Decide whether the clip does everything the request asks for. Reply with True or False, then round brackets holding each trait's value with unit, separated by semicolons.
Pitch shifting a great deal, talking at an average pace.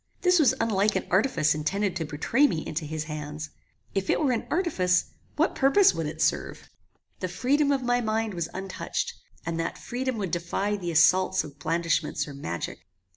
True (7.4 semitones; 180 wpm)